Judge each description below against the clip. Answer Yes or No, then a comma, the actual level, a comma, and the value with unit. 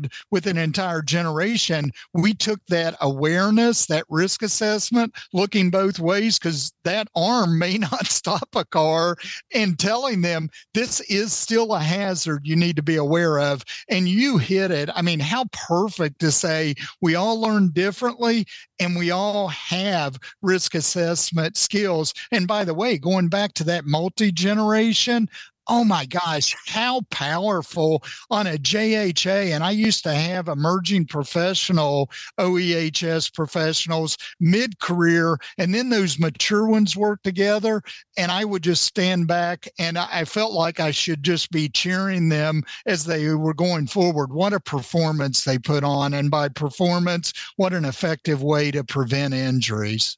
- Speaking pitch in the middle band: Yes, medium, 175 Hz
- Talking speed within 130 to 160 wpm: Yes, average, 155 wpm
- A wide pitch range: No, average, 4.1 semitones